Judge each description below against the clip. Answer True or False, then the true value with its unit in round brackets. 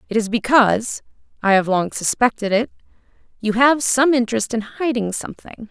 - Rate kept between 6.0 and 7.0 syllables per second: False (5.5 syllables/s)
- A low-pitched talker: False (230 Hz)